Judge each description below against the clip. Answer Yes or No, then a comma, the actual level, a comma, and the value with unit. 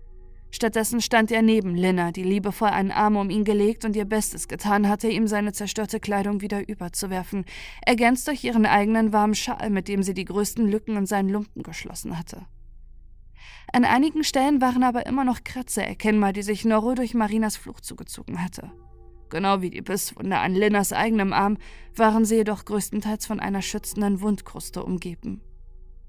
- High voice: Yes, high, 210 Hz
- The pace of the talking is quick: No, average, 170 wpm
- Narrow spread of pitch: Yes, narrow, 2.1 semitones